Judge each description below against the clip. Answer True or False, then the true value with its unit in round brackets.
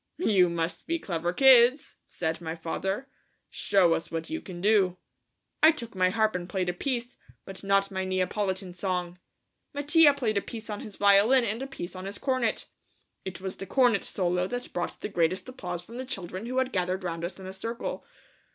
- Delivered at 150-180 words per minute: False (195 wpm)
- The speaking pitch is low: False (195 Hz)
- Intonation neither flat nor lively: True (4.8 semitones)